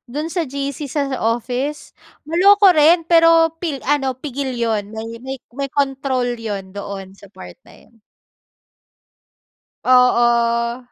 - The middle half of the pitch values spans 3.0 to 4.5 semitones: Yes, average, 4.2 semitones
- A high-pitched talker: Yes, very high, 260 Hz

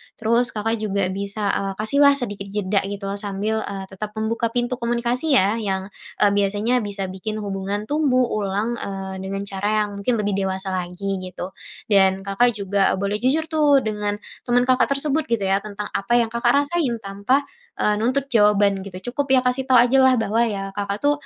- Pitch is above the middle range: Yes, high, 210 Hz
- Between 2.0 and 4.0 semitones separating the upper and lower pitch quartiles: Yes, average, 3.5 semitones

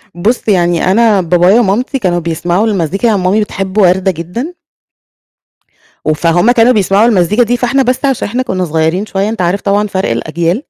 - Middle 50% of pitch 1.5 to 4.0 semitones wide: No, average, 4.5 semitones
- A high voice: Yes, high, 195 Hz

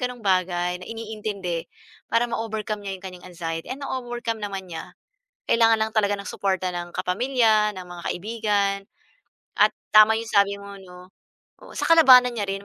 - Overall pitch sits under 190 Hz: No, high, 205 Hz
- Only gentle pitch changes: No, average, 3.5 semitones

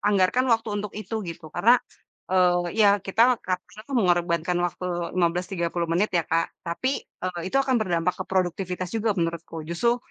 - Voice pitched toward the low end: No, medium, 185 Hz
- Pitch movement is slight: No, average, 4.2 semitones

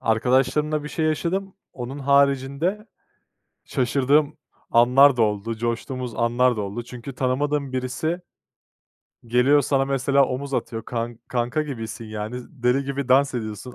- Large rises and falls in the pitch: No, average, 2.9 semitones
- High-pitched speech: No, low, 130 Hz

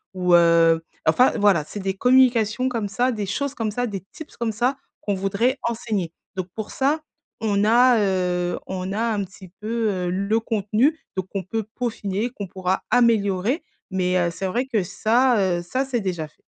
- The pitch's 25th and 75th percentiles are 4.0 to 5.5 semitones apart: Yes, average, 4.3 semitones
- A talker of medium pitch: No, high, 210 Hz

